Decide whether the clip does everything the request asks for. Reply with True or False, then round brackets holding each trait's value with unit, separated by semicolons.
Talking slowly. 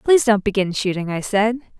False (200 wpm)